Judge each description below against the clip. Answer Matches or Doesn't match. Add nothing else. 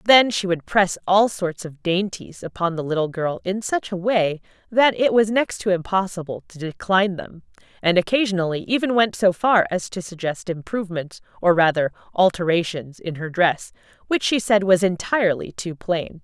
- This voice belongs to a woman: Matches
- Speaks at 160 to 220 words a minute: Matches